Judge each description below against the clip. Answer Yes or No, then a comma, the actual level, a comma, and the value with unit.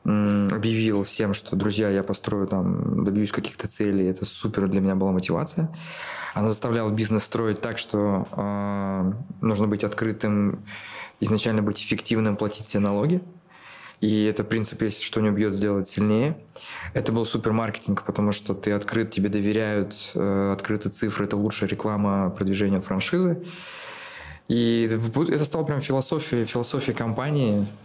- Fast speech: No, average, 145 wpm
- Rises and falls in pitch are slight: Yes, narrow, 2.3 semitones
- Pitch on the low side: Yes, low, 105 Hz